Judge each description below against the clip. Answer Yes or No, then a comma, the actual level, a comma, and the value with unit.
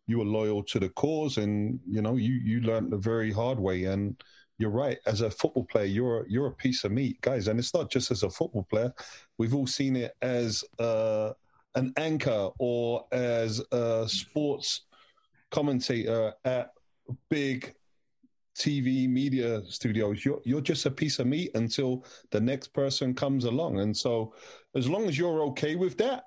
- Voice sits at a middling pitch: No, low, 125 Hz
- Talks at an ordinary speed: Yes, average, 180 wpm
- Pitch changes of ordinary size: Yes, average, 3.8 semitones